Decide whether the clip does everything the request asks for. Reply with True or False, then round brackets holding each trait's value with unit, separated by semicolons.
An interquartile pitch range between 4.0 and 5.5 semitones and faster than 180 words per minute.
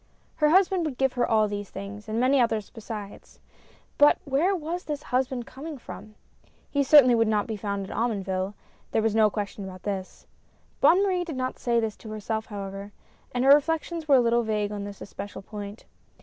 True (5.2 semitones; 200 wpm)